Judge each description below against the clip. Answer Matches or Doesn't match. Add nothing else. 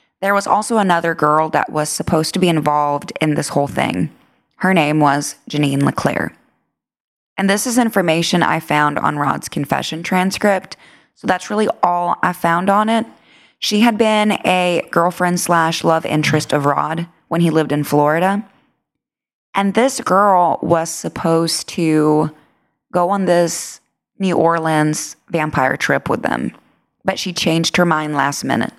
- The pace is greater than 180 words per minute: Doesn't match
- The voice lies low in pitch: Doesn't match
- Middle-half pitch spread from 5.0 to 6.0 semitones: Doesn't match